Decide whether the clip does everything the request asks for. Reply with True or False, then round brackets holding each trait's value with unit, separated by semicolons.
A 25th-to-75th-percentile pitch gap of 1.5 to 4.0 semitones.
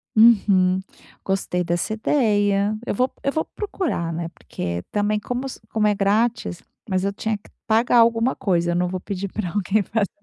True (3.5 semitones)